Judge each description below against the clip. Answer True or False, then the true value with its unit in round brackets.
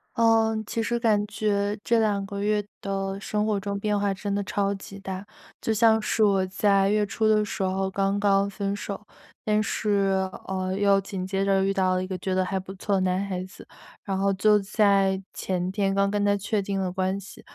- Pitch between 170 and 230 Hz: True (200 Hz)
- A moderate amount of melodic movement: False (1.4 semitones)